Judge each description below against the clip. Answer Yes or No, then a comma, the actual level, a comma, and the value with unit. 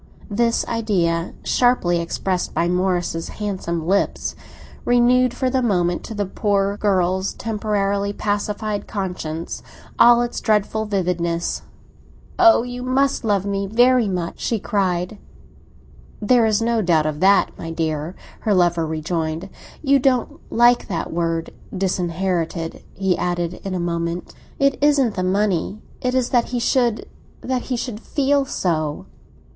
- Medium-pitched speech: No, high, 200 Hz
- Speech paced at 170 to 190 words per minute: No, slow, 135 wpm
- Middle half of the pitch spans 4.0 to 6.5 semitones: Yes, average, 5.2 semitones